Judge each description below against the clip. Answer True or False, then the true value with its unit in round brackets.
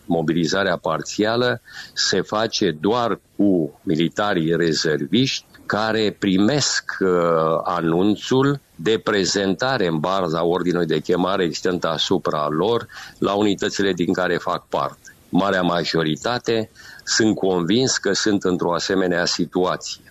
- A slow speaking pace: True (105 wpm)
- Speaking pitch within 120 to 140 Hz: False (95 Hz)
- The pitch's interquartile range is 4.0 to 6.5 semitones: False (3.4 semitones)